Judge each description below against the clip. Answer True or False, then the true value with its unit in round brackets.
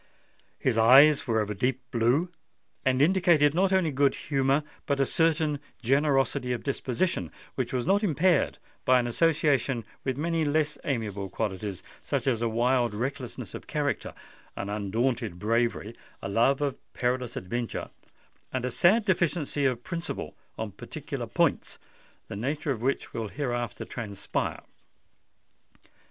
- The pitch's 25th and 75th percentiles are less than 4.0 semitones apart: False (4.3 semitones)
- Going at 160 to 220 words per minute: False (140 wpm)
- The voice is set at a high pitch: False (130 Hz)